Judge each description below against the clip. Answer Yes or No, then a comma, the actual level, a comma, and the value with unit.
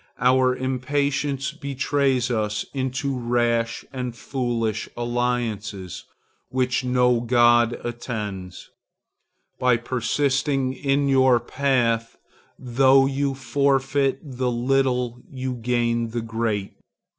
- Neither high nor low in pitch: No, low, 125 Hz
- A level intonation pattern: Yes, narrow, 2.2 semitones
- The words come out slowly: Yes, slow, 95 wpm